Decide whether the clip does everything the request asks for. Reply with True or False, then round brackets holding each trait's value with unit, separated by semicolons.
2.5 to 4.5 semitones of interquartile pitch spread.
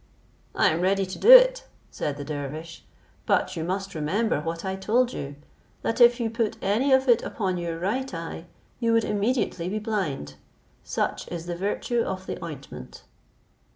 False (5.6 semitones)